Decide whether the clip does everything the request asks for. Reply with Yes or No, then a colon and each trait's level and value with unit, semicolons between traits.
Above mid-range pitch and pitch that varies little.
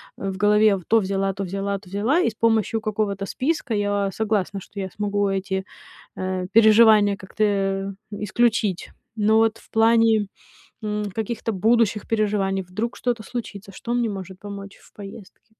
Yes: high, 205 Hz; narrow, 2.2 semitones